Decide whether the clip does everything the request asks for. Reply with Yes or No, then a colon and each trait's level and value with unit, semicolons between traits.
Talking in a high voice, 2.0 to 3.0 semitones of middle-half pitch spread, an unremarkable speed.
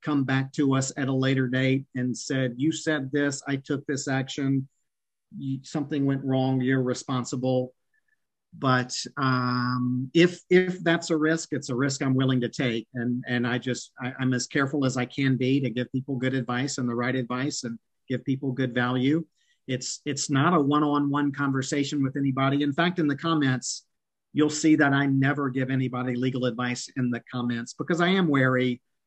No: low, 135 Hz; narrow, 2.4 semitones; average, 190 wpm